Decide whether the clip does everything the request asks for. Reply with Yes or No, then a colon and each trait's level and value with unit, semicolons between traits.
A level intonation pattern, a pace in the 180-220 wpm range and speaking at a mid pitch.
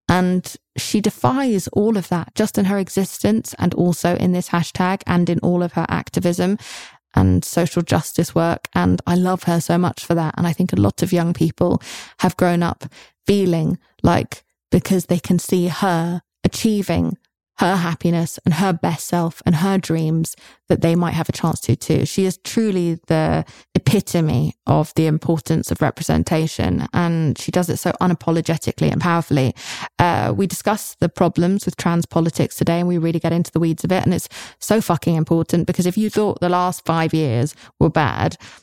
Yes: narrow, 2.0 semitones; average, 185 wpm; medium, 170 Hz